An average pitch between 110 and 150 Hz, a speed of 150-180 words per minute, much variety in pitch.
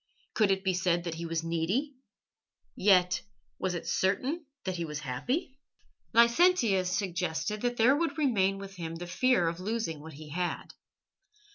No: high, 190 Hz; average, 160 wpm; wide, 5.7 semitones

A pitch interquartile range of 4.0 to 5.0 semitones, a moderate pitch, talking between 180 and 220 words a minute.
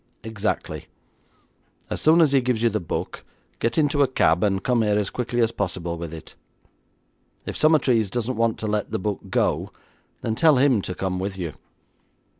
No: average, 4.7 semitones; low, 110 Hz; average, 185 wpm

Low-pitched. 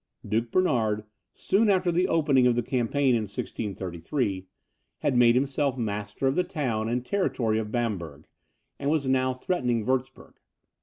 Yes: low, 125 Hz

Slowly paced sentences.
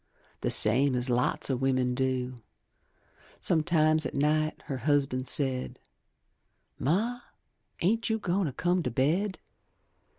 Yes: slow, 125 wpm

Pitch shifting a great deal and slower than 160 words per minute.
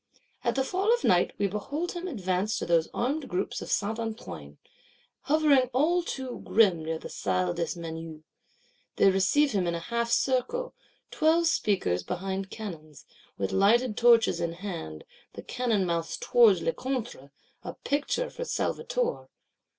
Yes: wide, 7.9 semitones; average, 150 wpm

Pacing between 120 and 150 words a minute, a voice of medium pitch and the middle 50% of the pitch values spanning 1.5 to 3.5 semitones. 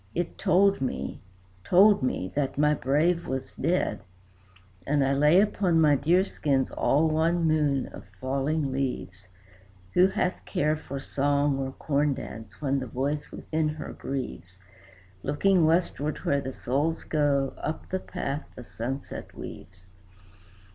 Yes: average, 140 wpm; medium, 145 Hz; average, 3.2 semitones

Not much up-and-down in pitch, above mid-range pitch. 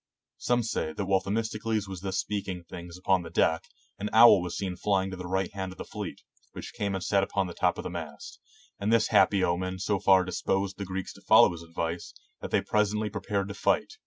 No: narrow, 2.1 semitones; very low, 95 Hz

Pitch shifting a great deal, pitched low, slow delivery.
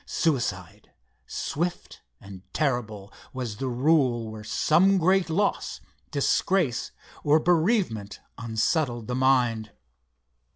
Yes: wide, 6.4 semitones; low, 130 Hz; slow, 95 wpm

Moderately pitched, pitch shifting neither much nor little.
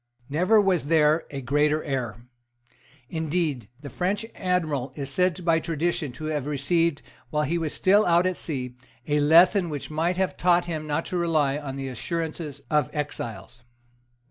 Yes: medium, 155 Hz; average, 3.4 semitones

